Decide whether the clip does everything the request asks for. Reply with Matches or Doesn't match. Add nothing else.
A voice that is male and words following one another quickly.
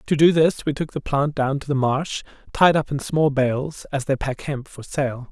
Matches